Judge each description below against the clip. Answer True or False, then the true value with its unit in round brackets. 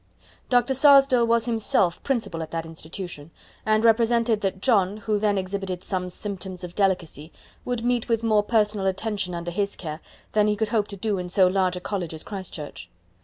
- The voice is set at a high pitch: True (200 Hz)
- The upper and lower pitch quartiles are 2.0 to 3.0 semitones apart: False (3.7 semitones)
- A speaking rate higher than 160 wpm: True (190 wpm)